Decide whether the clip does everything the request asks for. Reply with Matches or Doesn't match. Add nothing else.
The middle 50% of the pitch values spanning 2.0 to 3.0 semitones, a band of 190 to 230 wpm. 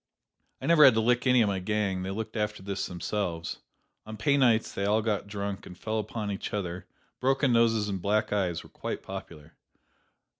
Matches